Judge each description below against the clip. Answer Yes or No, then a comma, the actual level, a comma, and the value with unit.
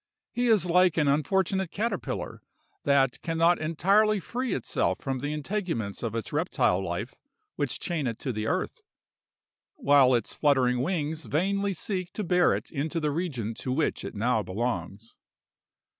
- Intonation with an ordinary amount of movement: No, wide, 6.7 semitones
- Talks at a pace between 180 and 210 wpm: No, average, 160 wpm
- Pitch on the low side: No, medium, 150 Hz